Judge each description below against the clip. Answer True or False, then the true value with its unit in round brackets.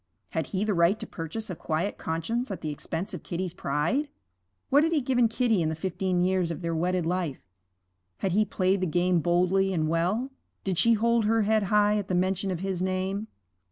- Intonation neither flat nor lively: True (3.6 semitones)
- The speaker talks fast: True (210 wpm)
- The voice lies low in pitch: False (185 Hz)